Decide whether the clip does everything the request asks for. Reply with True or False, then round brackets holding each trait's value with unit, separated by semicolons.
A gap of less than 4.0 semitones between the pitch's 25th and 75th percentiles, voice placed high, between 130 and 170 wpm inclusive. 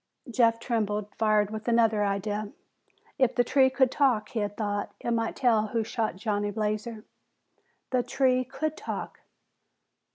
True (2.7 semitones; 225 Hz; 150 wpm)